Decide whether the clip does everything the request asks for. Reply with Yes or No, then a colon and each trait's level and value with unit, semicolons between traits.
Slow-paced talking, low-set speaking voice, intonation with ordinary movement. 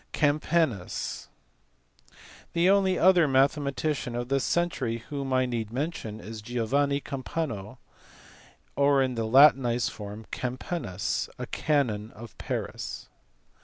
Yes: slow, 110 wpm; low, 130 Hz; average, 4.4 semitones